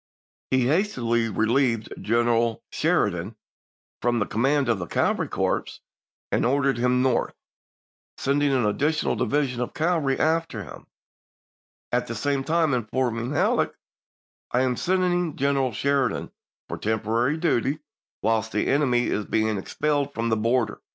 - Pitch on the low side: Yes, low, 125 Hz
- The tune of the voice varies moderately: Yes, average, 3.8 semitones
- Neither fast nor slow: Yes, average, 145 wpm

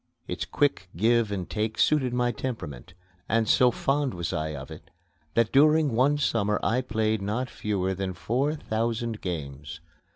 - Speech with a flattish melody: No, average, 4.9 semitones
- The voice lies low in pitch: Yes, low, 110 Hz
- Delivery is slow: No, average, 160 wpm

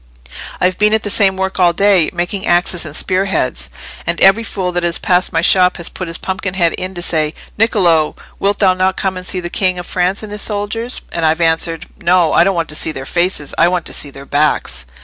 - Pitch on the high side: No, medium, 180 Hz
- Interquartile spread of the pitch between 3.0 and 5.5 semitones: No, narrow, 2.4 semitones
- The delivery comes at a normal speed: No, fast, 230 wpm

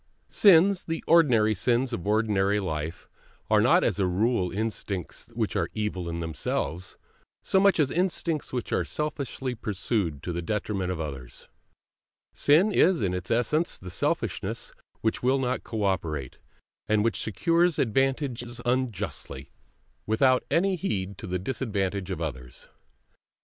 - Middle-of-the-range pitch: No, low, 110 Hz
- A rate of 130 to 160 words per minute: Yes, average, 140 wpm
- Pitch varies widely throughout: Yes, wide, 6.6 semitones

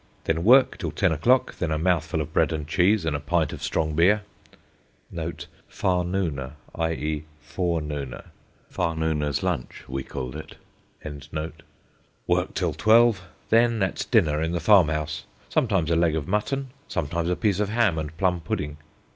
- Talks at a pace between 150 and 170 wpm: Yes, average, 155 wpm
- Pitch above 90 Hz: No, very low, 85 Hz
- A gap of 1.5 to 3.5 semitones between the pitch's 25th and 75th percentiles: No, average, 4.0 semitones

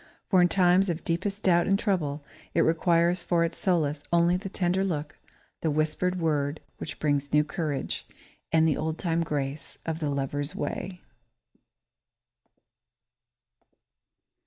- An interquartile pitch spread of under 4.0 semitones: Yes, average, 3.2 semitones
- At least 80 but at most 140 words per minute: Yes, slow, 135 wpm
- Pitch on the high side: No, medium, 165 Hz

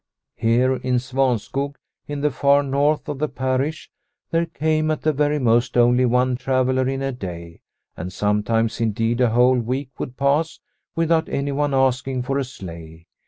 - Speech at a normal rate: Yes, average, 165 wpm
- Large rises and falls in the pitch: No, average, 3.0 semitones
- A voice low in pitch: Yes, low, 130 Hz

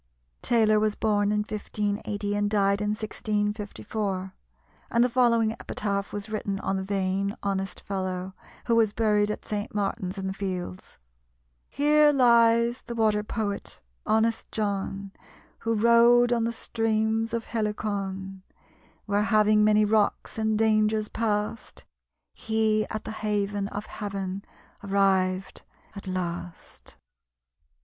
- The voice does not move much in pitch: Yes, narrow, 1.9 semitones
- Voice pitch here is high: Yes, high, 210 Hz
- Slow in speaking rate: Yes, slow, 125 wpm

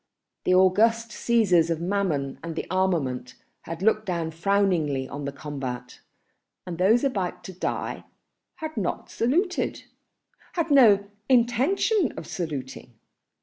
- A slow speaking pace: Yes, slow, 120 wpm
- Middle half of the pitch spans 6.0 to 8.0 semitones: Yes, wide, 6.5 semitones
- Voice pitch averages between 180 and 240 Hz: Yes, medium, 185 Hz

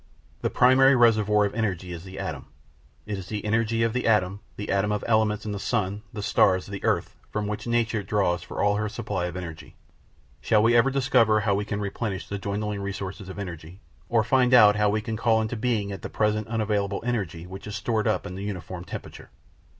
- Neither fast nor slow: No, fast, 210 wpm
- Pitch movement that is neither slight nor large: No, narrow, 2.2 semitones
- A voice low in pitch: Yes, low, 105 Hz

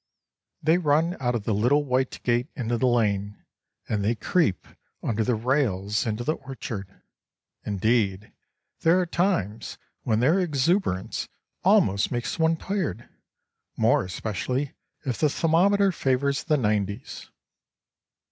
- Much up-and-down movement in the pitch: Yes, wide, 6.5 semitones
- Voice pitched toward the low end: Yes, low, 125 Hz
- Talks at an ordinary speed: No, slow, 130 wpm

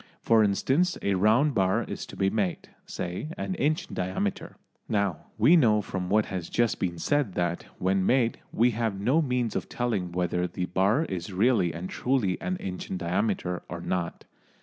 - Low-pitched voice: Yes, low, 100 Hz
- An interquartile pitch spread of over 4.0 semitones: Yes, average, 5.1 semitones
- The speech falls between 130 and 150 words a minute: No, average, 185 wpm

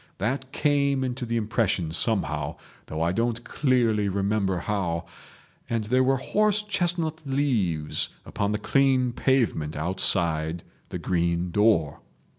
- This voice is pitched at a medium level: No, low, 110 Hz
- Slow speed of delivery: Yes, slow, 125 wpm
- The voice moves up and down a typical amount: No, wide, 7.2 semitones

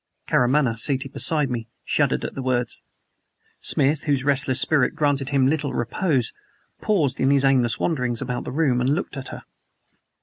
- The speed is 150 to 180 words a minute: Yes, average, 165 wpm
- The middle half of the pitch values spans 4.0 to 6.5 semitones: No, narrow, 2.6 semitones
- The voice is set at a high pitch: No, low, 135 Hz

